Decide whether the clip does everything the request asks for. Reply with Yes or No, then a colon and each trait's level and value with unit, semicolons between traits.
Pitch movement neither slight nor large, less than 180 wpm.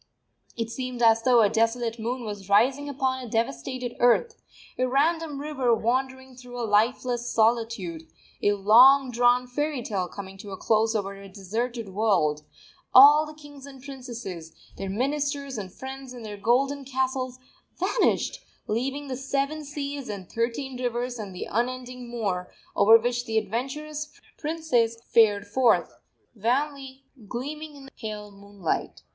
Yes: average, 3.7 semitones; average, 150 wpm